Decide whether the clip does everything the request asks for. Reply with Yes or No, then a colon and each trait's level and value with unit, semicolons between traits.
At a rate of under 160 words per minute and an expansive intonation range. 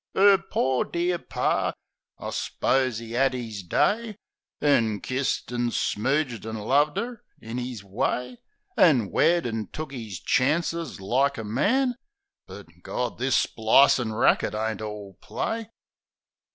Yes: average, 140 wpm; wide, 5.9 semitones